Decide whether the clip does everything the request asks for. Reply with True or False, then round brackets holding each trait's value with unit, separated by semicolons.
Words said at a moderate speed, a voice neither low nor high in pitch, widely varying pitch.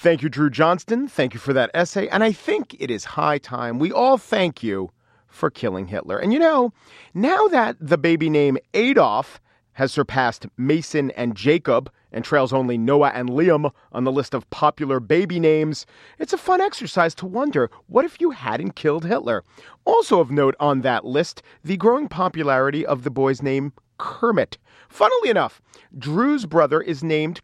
True (180 wpm; 155 Hz; 6.1 semitones)